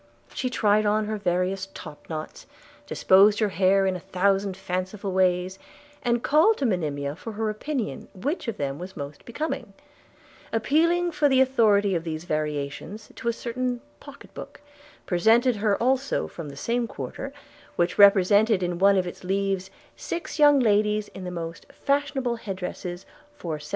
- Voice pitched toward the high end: Yes, high, 200 Hz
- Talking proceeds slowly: No, average, 160 wpm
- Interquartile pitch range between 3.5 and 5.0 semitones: Yes, average, 4.7 semitones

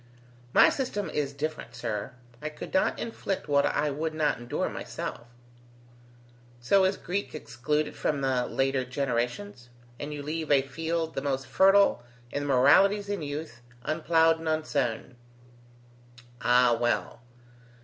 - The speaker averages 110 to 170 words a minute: Yes, average, 140 wpm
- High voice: No, medium, 150 Hz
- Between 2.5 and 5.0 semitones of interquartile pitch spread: Yes, average, 4.0 semitones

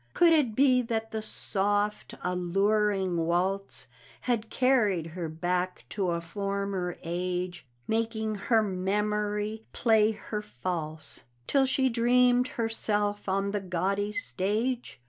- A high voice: Yes, high, 205 Hz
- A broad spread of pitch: No, average, 3.5 semitones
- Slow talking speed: Yes, slow, 120 wpm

